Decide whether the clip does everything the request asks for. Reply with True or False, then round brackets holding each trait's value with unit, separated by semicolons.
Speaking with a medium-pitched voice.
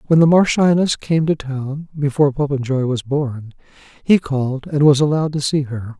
True (145 Hz)